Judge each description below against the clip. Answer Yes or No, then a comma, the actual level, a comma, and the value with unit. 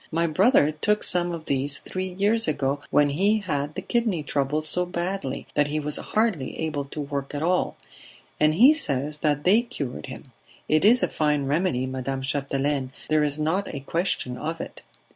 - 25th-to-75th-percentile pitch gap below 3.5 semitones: No, average, 4.4 semitones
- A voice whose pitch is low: No, medium, 155 Hz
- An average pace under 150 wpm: No, average, 185 wpm